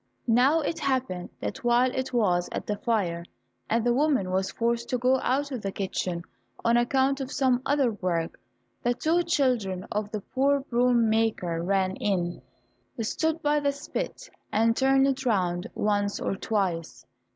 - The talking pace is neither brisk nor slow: Yes, average, 165 wpm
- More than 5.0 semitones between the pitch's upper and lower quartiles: Yes, wide, 5.6 semitones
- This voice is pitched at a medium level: No, high, 235 Hz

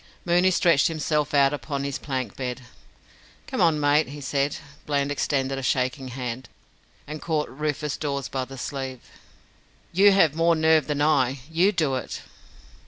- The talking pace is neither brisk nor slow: Yes, average, 160 wpm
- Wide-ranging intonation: No, average, 2.8 semitones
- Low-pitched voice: No, medium, 145 Hz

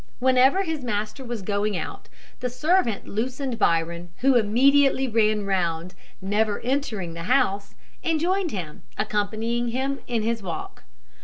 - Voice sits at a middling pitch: No, high, 230 Hz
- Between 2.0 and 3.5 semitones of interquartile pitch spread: No, average, 4.7 semitones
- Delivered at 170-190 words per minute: No, average, 140 wpm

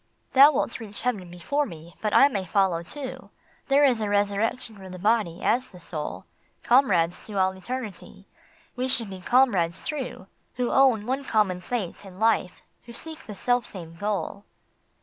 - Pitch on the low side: No, high, 210 Hz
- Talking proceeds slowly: No, average, 175 wpm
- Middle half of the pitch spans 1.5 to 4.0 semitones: No, average, 5.1 semitones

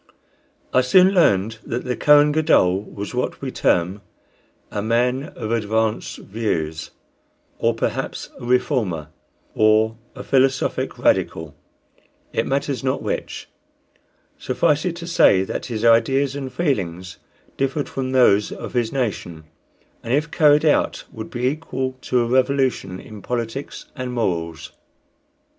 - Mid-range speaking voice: No, low, 125 Hz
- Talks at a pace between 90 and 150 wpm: Yes, slow, 135 wpm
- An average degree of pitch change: Yes, average, 4.6 semitones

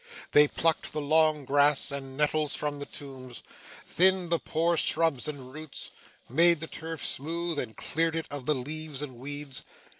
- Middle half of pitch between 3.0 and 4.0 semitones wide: No, narrow, 2.5 semitones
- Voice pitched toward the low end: No, medium, 150 Hz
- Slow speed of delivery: No, average, 170 wpm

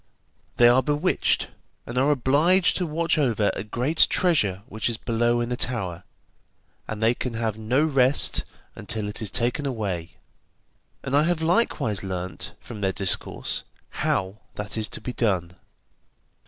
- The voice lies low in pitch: Yes, low, 120 Hz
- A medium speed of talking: Yes, average, 155 wpm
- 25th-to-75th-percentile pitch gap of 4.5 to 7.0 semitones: Yes, average, 5.3 semitones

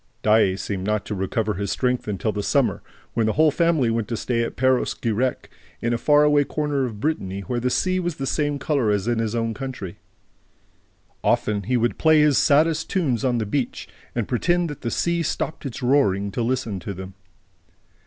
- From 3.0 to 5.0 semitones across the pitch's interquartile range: No, wide, 5.5 semitones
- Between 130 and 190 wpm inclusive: No, fast, 205 wpm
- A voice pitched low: Yes, low, 120 Hz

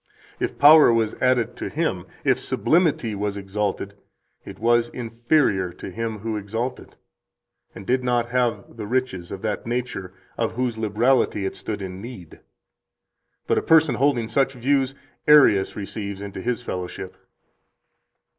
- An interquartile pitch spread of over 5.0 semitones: No, average, 3.9 semitones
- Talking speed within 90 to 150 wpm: Yes, average, 145 wpm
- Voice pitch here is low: Yes, low, 115 Hz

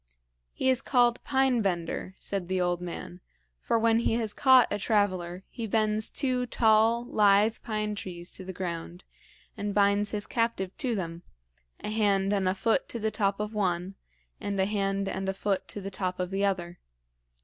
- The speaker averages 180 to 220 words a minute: Yes, average, 185 wpm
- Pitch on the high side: Yes, high, 205 Hz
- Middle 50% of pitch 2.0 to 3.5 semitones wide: Yes, average, 3.0 semitones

